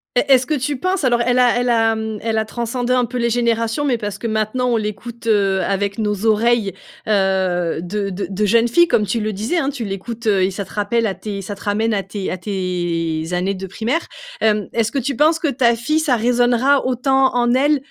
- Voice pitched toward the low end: No, high, 225 Hz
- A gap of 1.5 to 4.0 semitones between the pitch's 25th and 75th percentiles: Yes, average, 3.7 semitones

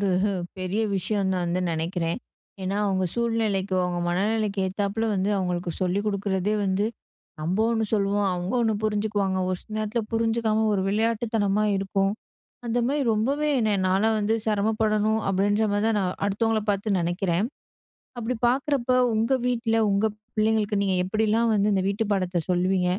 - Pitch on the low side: No, high, 205 Hz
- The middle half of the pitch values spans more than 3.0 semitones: No, average, 2.7 semitones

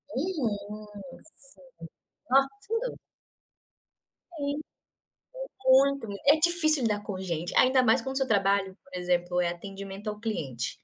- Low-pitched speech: No, high, 220 Hz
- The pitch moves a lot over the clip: Yes, wide, 6.1 semitones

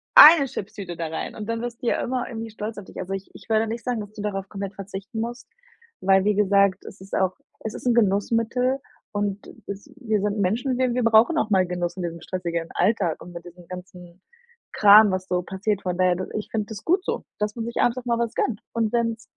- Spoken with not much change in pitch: No, average, 3.6 semitones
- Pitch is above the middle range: Yes, high, 210 Hz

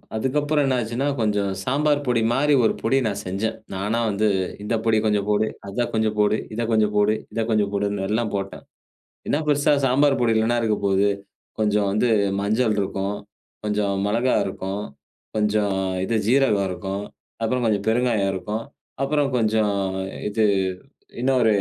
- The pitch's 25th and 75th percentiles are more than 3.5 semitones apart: No, average, 3.2 semitones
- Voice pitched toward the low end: Yes, low, 110 Hz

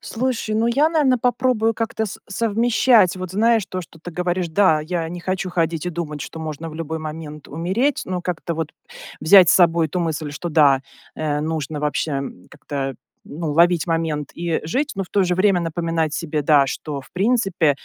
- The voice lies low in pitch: No, medium, 170 Hz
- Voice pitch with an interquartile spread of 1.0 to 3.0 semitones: No, average, 4.1 semitones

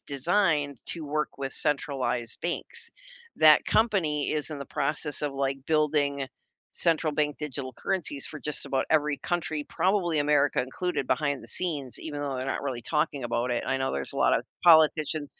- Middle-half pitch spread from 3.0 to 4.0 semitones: No, narrow, 2.4 semitones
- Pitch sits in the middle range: Yes, medium, 150 Hz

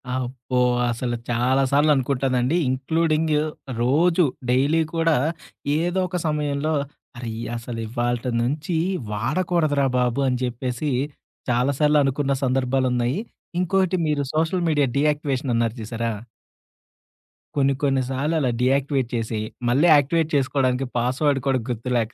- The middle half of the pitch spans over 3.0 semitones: Yes, average, 3.4 semitones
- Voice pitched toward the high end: No, low, 135 Hz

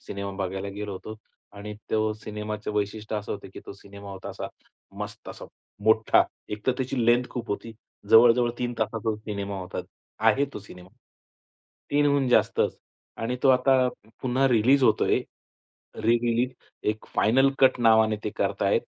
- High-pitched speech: No, low, 110 Hz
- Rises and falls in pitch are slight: No, average, 3.1 semitones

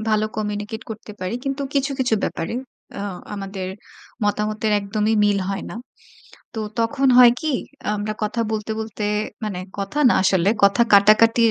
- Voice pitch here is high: Yes, high, 215 Hz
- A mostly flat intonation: Yes, narrow, 2.2 semitones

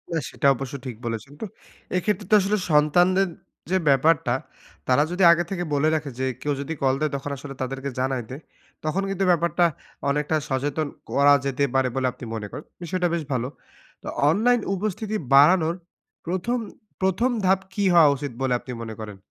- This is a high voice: No, medium, 150 Hz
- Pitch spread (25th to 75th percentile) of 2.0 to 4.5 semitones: No, wide, 5.4 semitones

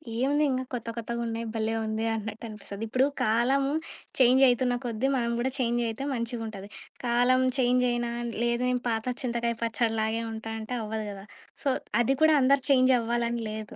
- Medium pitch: No, high, 235 Hz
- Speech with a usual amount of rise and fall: No, narrow, 2.2 semitones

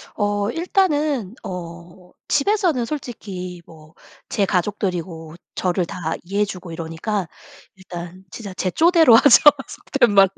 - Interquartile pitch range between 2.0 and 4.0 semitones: No, wide, 5.4 semitones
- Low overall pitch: No, high, 195 Hz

